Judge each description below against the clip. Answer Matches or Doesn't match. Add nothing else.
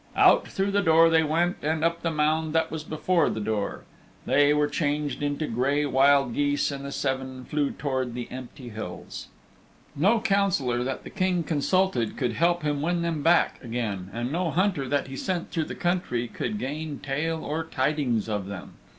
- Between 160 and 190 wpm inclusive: Matches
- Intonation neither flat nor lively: Matches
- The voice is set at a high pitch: Doesn't match